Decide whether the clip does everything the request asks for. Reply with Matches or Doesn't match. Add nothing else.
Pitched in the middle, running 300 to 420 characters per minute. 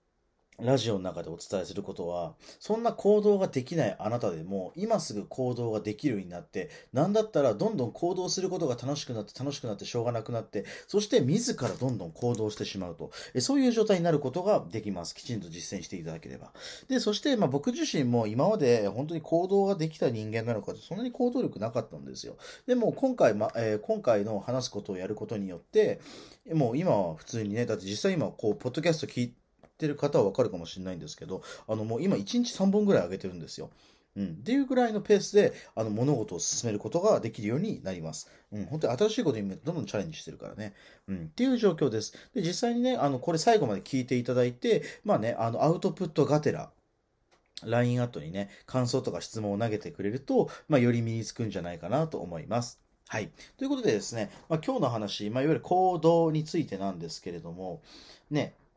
Doesn't match